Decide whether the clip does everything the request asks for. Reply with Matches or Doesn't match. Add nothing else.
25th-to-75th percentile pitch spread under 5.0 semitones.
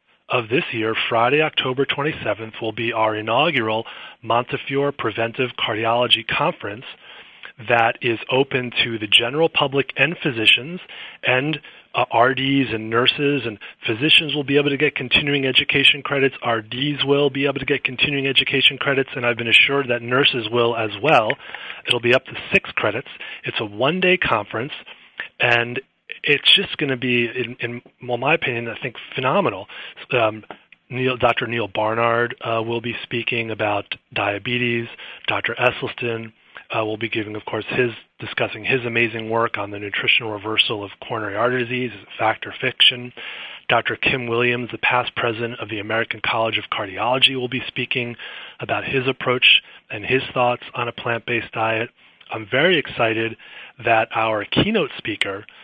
Matches